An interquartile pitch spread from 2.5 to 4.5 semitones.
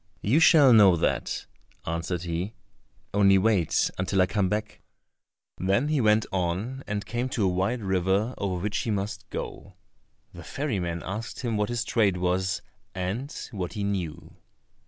Yes: average, 3.4 semitones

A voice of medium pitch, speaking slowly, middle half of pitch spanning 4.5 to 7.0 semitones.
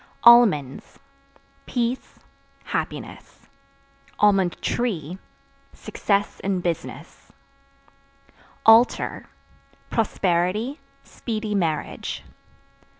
No: high, 205 Hz; slow, 50 wpm; average, 5.2 semitones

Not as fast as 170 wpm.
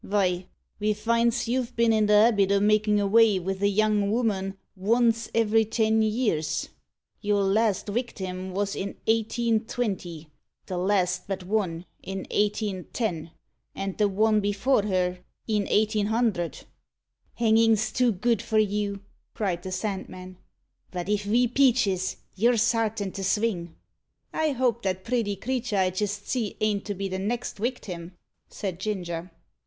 Yes: average, 140 wpm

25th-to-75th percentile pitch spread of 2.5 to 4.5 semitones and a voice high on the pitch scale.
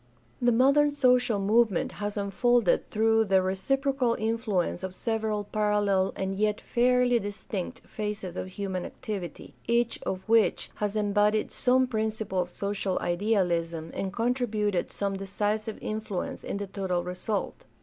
Yes: average, 3.0 semitones; high, 210 Hz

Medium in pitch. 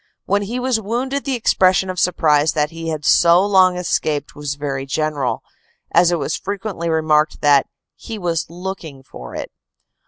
Yes: medium, 170 Hz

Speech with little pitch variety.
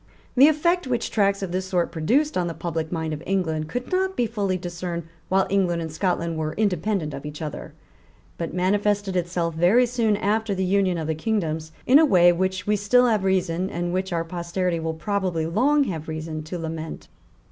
No: average, 3.9 semitones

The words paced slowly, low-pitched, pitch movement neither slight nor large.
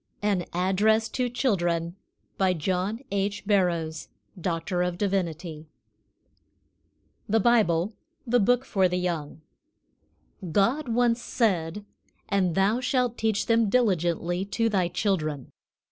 No: slow, 105 wpm; high, 195 Hz; average, 4.4 semitones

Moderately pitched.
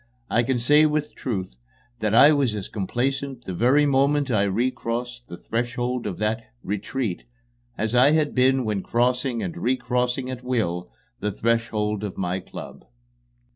No: low, 120 Hz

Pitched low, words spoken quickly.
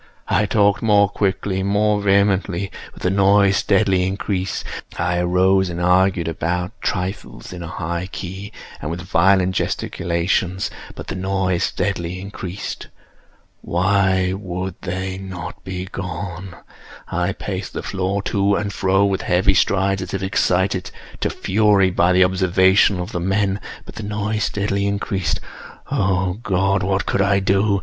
No: very low, 95 Hz; average, 140 wpm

